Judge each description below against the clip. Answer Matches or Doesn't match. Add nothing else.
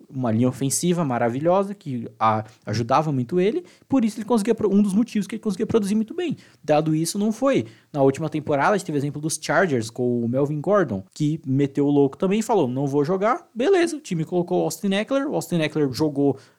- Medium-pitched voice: Matches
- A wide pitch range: Matches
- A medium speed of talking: Doesn't match